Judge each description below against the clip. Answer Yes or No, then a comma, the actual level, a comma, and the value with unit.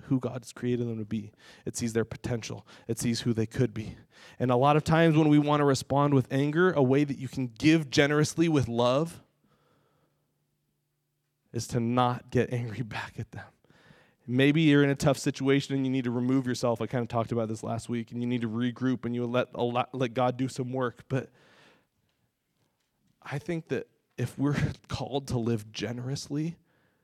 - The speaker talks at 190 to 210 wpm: Yes, average, 195 wpm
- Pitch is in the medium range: No, low, 125 Hz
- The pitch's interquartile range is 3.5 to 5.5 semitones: No, average, 3.1 semitones